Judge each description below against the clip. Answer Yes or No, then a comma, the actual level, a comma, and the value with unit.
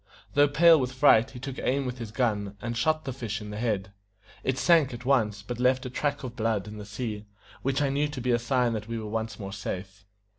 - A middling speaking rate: No, fast, 250 wpm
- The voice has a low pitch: Yes, low, 120 Hz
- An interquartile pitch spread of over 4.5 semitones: No, average, 3.9 semitones